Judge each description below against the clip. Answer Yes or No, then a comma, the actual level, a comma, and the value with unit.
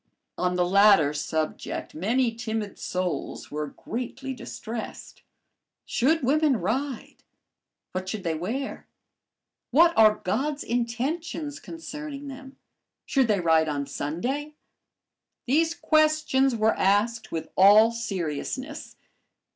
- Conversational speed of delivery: No, slow, 105 wpm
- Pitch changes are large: Yes, wide, 7.0 semitones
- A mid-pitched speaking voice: No, high, 230 Hz